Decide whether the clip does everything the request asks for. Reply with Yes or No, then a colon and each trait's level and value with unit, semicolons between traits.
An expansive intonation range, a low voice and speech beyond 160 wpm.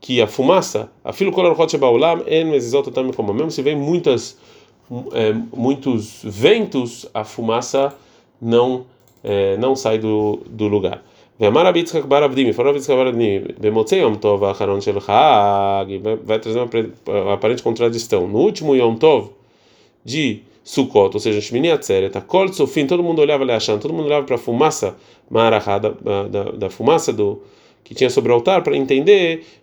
Yes: wide, 6.5 semitones; low, 130 Hz; average, 170 wpm